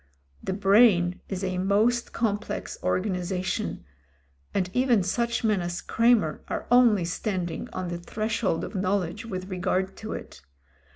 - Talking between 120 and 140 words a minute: Yes, slow, 135 wpm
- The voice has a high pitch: Yes, high, 195 Hz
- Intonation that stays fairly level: No, average, 3.3 semitones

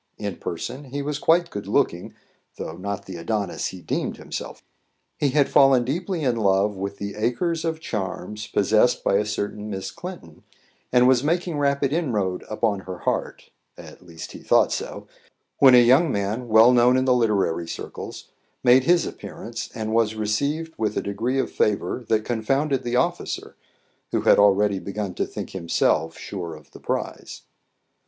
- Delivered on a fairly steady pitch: No, average, 5.3 semitones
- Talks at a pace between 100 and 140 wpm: No, average, 170 wpm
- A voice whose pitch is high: No, low, 110 Hz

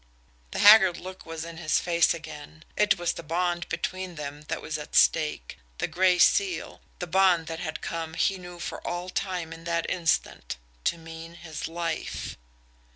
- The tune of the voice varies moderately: No, narrow, 1.8 semitones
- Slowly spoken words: No, average, 175 wpm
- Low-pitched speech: No, medium, 170 Hz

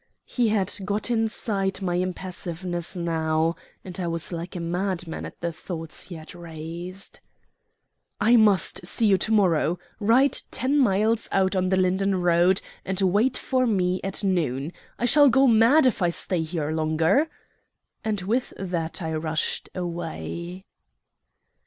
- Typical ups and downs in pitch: Yes, average, 3.6 semitones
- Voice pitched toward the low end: No, medium, 185 Hz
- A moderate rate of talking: Yes, average, 150 wpm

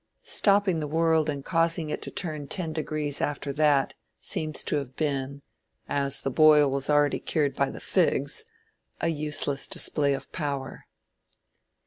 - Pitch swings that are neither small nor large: No, narrow, 2.1 semitones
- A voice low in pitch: No, medium, 150 Hz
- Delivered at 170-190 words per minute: No, average, 155 wpm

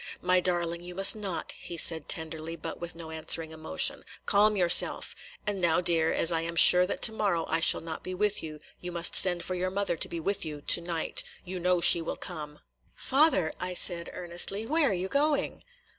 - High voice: No, medium, 175 Hz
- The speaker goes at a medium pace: No, fast, 210 wpm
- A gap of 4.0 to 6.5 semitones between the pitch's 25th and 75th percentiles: No, narrow, 2.6 semitones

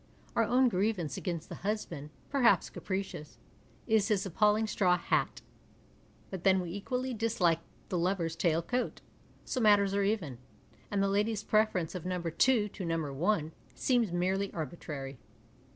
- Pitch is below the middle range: No, high, 195 Hz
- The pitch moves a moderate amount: Yes, average, 4.1 semitones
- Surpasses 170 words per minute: No, average, 150 wpm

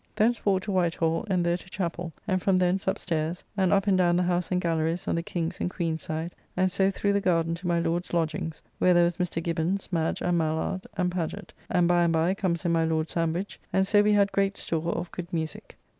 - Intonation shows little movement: Yes, narrow, 2.1 semitones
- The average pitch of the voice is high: No, medium, 175 Hz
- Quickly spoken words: Yes, fast, 245 wpm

